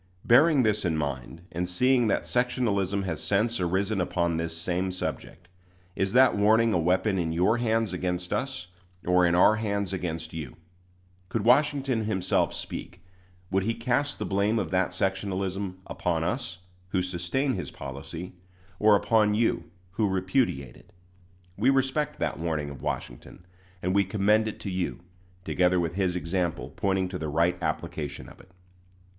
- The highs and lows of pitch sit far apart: No, average, 4.0 semitones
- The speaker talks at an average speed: Yes, average, 160 wpm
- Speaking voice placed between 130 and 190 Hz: No, very low, 95 Hz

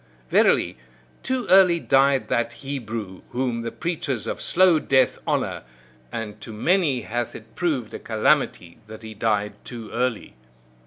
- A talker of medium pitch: No, low, 120 Hz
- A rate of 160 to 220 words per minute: No, average, 145 wpm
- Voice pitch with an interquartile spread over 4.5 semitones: Yes, average, 5.1 semitones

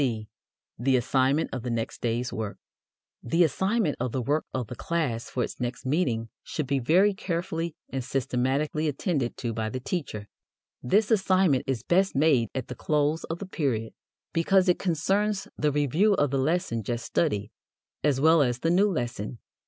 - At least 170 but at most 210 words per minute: Yes, average, 175 wpm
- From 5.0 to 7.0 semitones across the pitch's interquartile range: Yes, wide, 5.5 semitones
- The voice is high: No, medium, 140 Hz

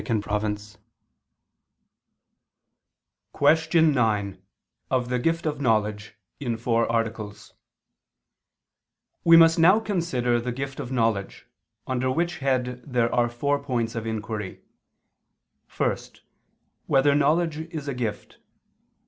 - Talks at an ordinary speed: No, slow, 105 wpm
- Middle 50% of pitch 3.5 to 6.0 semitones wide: Yes, average, 4.6 semitones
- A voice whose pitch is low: Yes, low, 125 Hz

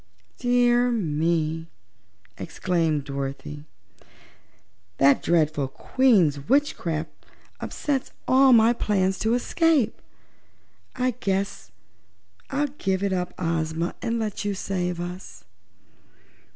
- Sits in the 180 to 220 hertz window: Yes, medium, 185 Hz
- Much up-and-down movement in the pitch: Yes, wide, 7.1 semitones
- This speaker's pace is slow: Yes, slow, 95 wpm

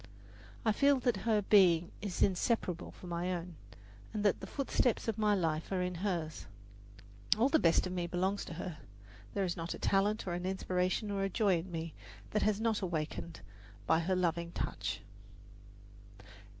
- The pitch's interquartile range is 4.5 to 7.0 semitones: No, average, 3.4 semitones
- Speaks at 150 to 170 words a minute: No, average, 180 wpm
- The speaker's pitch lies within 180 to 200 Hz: Yes, medium, 185 Hz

